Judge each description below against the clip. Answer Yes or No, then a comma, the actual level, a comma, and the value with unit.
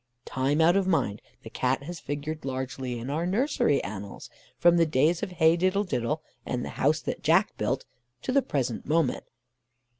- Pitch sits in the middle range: Yes, medium, 150 Hz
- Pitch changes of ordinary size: Yes, average, 4.9 semitones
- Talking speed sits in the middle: Yes, average, 180 wpm